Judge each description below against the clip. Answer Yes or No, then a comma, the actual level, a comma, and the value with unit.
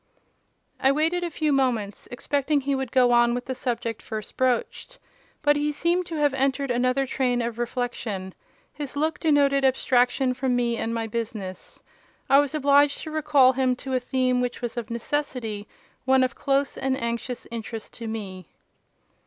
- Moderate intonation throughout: Yes, average, 3.0 semitones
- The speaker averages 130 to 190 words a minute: Yes, average, 170 wpm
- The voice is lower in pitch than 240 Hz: No, very high, 255 Hz